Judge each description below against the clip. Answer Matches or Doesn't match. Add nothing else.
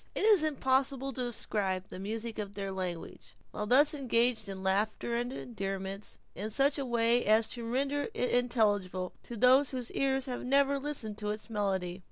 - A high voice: Matches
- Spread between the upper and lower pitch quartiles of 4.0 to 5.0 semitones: Matches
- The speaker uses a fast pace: Doesn't match